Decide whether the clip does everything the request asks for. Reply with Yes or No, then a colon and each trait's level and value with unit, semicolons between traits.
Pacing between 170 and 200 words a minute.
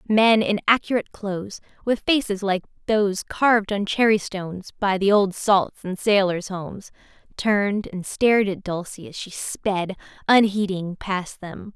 No: average, 155 wpm